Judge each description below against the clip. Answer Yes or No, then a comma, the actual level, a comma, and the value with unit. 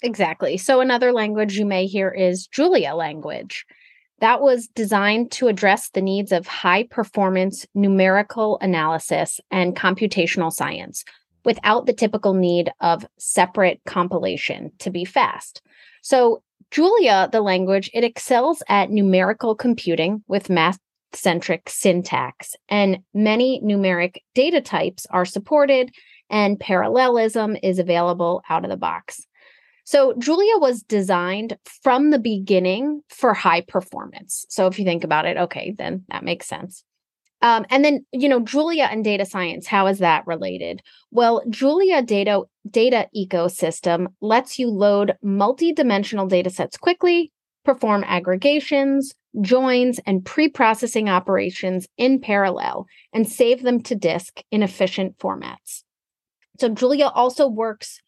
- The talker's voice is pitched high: Yes, high, 210 Hz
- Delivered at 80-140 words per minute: Yes, slow, 135 wpm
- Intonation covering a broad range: No, average, 5.0 semitones